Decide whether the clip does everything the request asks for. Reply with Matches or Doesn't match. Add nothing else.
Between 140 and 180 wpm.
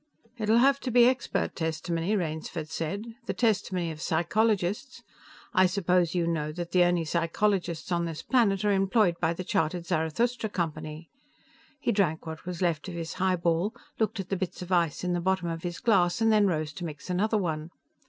Doesn't match